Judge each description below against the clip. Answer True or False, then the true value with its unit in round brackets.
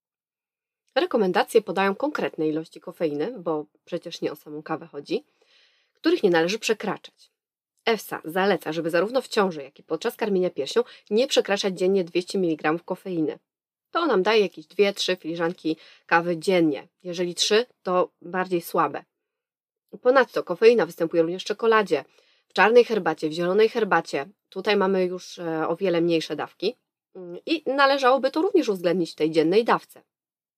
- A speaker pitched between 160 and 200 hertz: True (185 Hz)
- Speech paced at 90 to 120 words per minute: False (145 wpm)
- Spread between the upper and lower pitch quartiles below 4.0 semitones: False (5.5 semitones)